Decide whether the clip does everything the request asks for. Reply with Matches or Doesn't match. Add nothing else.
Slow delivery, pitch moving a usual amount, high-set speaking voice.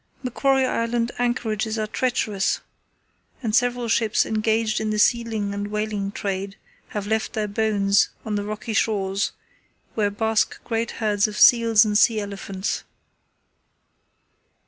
Doesn't match